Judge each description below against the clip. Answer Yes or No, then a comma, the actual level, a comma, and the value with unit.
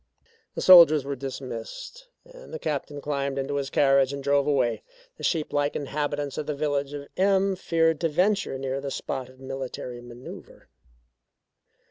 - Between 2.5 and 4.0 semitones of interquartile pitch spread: Yes, average, 3.2 semitones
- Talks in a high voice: No, medium, 140 Hz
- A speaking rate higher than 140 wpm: Yes, average, 160 wpm